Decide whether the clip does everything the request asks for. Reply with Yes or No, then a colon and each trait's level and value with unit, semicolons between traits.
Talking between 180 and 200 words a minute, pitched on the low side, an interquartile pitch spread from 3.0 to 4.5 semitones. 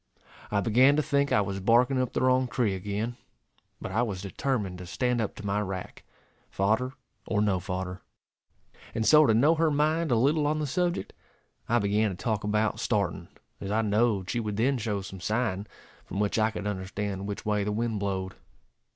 Yes: average, 195 wpm; low, 110 Hz; average, 4.0 semitones